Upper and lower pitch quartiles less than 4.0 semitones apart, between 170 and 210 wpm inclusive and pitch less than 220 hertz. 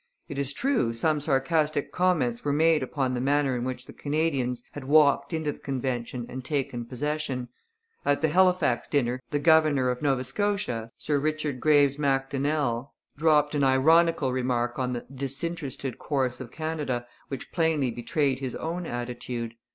No: average, 3.4 semitones; average, 160 wpm; medium, 140 Hz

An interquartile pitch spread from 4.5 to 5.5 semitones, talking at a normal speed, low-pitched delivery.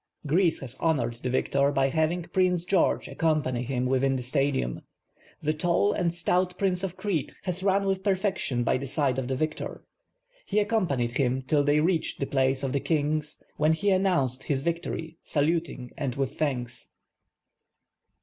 No: average, 5.1 semitones; average, 170 wpm; medium, 150 Hz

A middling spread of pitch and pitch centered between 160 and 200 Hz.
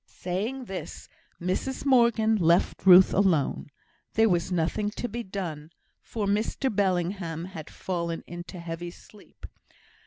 Yes: average, 3.9 semitones; medium, 185 Hz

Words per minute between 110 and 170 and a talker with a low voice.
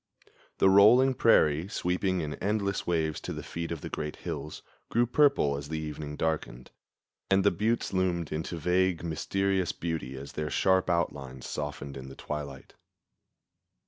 Yes: average, 155 wpm; very low, 85 Hz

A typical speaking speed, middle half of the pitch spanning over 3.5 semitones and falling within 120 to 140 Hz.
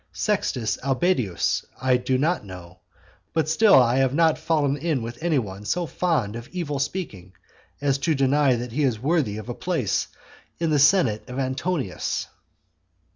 Yes: average, 165 wpm; average, 5.3 semitones; low, 135 Hz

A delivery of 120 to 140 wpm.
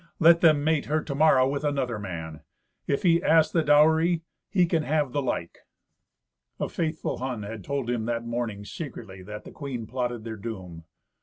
No: average, 180 wpm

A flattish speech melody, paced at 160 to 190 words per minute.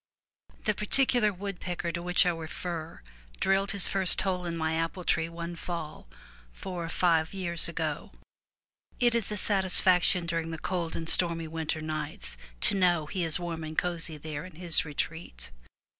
Yes: narrow, 2.2 semitones; average, 170 wpm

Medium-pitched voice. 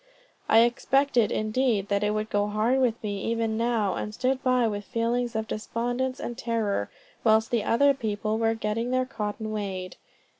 No: high, 225 Hz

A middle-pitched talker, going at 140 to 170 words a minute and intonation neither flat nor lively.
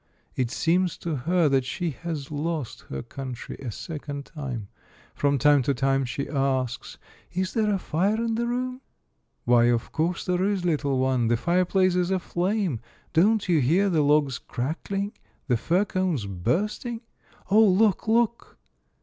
No: medium, 165 Hz; average, 165 wpm; wide, 6.0 semitones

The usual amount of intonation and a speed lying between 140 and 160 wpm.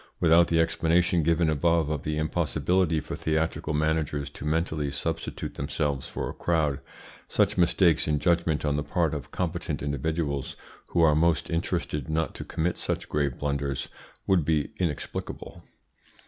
No: narrow, 2.3 semitones; average, 150 wpm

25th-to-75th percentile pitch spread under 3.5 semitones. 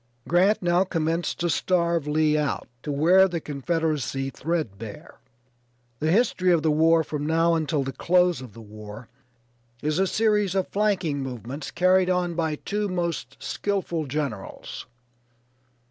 No: average, 4.0 semitones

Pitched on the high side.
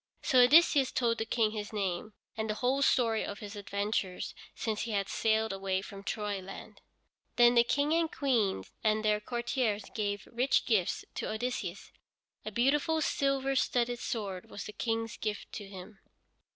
Yes: high, 220 Hz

